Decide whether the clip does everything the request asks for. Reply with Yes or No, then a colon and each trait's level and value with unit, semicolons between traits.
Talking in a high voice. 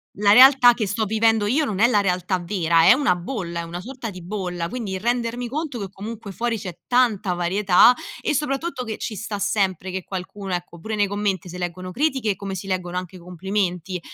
Yes: high, 200 Hz